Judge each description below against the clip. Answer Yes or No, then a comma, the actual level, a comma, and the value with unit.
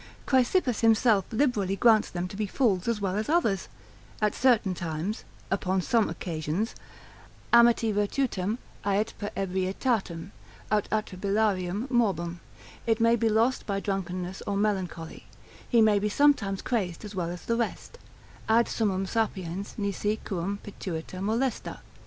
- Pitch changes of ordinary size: Yes, average, 3.3 semitones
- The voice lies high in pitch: Yes, high, 205 Hz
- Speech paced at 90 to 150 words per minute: Yes, average, 140 wpm